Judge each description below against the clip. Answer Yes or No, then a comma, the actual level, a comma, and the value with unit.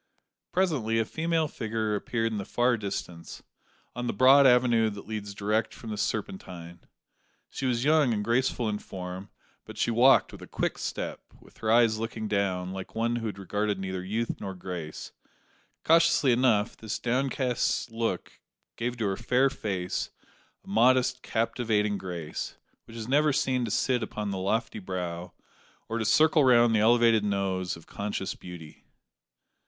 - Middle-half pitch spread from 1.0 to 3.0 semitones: No, average, 3.7 semitones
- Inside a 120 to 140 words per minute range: No, average, 160 wpm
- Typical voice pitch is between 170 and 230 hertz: No, low, 110 Hz